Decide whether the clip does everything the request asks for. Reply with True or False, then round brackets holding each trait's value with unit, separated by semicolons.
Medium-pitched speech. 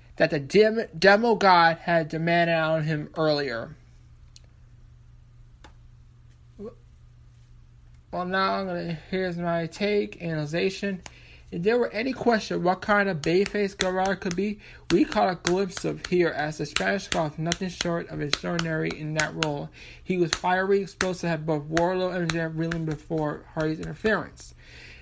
True (170 Hz)